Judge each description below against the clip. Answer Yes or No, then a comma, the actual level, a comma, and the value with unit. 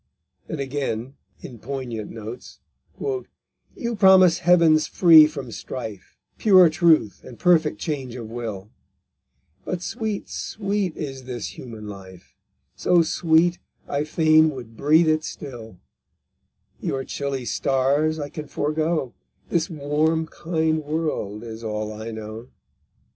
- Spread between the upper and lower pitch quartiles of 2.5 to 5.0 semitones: No, wide, 5.6 semitones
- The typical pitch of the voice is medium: Yes, medium, 145 Hz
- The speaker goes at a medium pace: No, slow, 120 wpm